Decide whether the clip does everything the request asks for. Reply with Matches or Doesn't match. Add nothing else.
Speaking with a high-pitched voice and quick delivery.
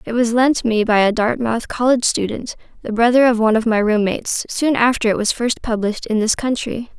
Matches